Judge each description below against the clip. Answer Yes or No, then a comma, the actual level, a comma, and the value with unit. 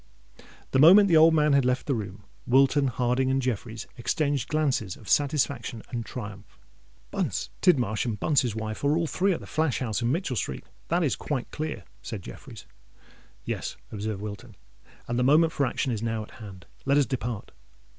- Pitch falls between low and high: No, low, 130 Hz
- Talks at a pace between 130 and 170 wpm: No, average, 180 wpm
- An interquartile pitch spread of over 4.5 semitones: Yes, average, 5.0 semitones